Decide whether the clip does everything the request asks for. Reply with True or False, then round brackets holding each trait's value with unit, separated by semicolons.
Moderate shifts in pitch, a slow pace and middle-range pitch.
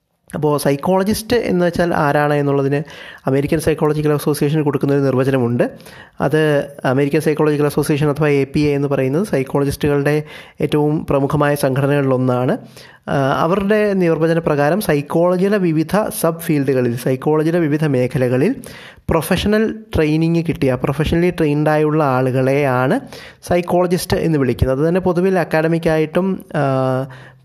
False (3.0 semitones; 105 wpm; 150 Hz)